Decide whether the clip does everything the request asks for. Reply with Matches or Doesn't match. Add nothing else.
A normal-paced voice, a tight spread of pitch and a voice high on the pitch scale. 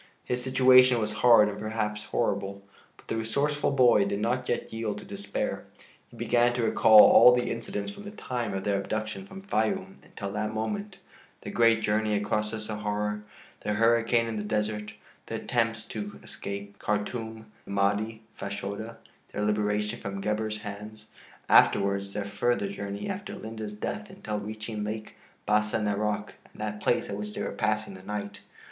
Doesn't match